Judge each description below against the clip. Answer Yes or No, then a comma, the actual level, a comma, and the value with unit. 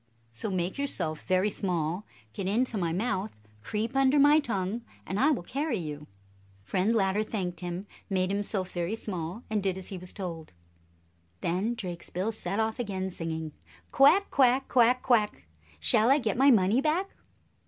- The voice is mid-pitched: No, high, 200 Hz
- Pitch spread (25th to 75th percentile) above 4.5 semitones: Yes, average, 5.1 semitones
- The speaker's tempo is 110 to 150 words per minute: No, average, 165 wpm